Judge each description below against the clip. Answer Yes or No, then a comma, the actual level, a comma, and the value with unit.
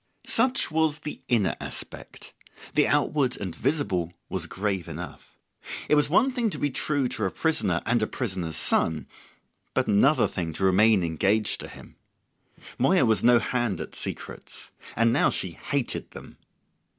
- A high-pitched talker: No, low, 115 Hz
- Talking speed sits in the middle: Yes, average, 160 wpm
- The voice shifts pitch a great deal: Yes, wide, 7.6 semitones